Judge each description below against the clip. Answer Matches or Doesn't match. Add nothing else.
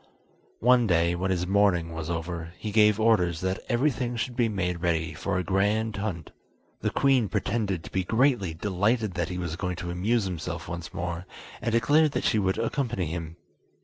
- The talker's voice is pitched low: Matches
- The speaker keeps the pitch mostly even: Doesn't match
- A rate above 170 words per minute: Matches